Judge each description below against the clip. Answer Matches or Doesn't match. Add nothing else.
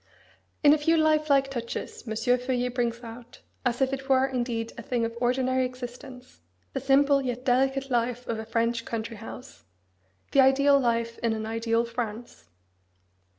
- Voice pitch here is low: Doesn't match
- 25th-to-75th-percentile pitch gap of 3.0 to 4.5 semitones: Doesn't match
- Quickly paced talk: Doesn't match